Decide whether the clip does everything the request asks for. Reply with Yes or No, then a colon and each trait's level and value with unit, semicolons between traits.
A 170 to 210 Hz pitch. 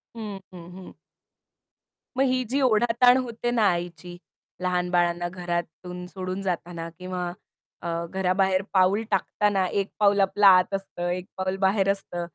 Yes: medium, 185 Hz